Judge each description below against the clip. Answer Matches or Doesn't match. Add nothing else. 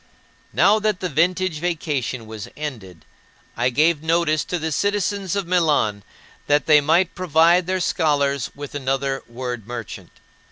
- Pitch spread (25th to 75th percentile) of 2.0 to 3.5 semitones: Doesn't match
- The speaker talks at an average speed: Matches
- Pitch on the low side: Doesn't match